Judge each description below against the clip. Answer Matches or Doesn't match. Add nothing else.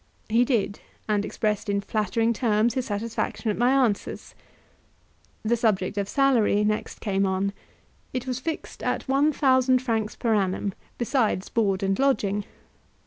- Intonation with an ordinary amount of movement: Matches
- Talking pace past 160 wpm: Doesn't match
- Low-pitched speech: Doesn't match